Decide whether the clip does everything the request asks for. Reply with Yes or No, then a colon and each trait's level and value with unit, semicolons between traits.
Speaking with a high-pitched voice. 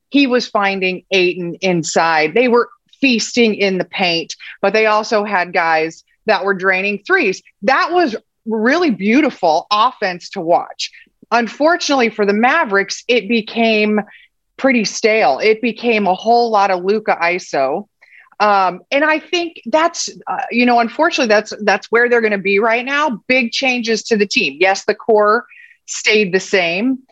Yes: high, 220 Hz